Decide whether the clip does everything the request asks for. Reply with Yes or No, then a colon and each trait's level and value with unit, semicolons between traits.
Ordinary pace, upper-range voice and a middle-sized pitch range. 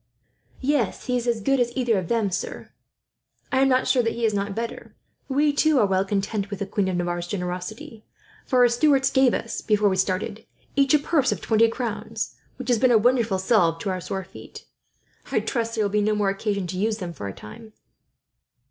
No: fast, 220 wpm; high, 220 Hz; average, 4.2 semitones